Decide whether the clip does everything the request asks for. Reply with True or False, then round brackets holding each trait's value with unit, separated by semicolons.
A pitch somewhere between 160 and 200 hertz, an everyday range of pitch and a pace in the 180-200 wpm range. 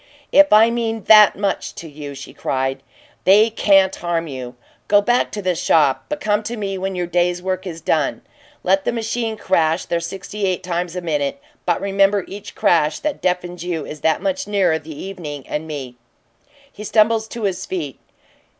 True (185 Hz; 4.6 semitones; 185 wpm)